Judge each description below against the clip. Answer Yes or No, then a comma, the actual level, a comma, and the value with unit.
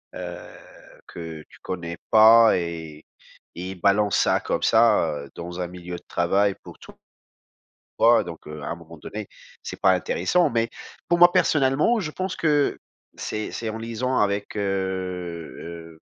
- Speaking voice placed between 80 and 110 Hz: Yes, very low, 95 Hz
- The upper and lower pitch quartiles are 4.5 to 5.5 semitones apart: Yes, average, 5.1 semitones